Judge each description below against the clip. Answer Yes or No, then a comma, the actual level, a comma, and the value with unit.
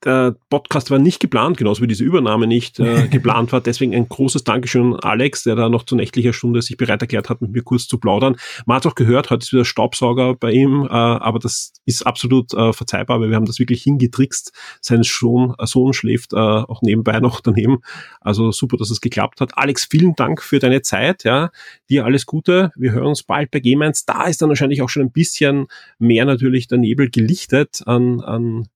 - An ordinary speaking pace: No, fast, 215 wpm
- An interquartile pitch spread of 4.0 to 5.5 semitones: No, narrow, 2.5 semitones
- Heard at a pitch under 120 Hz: No, low, 125 Hz